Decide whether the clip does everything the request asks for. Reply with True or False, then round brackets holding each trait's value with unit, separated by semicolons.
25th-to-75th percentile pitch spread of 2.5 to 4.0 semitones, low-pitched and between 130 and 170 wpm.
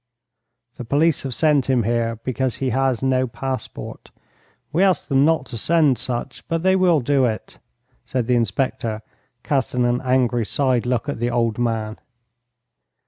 True (2.9 semitones; 130 Hz; 160 wpm)